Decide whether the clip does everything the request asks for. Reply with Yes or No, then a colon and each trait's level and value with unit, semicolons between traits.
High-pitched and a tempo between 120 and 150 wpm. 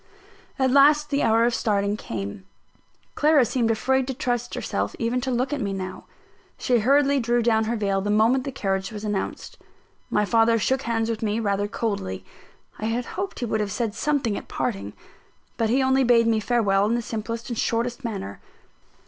No: high, 230 Hz; average, 190 wpm